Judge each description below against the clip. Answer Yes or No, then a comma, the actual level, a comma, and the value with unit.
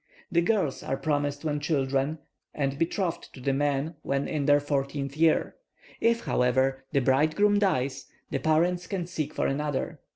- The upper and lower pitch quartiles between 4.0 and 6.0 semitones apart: No, average, 3.2 semitones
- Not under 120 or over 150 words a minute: No, average, 160 wpm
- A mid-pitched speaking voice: Yes, medium, 145 Hz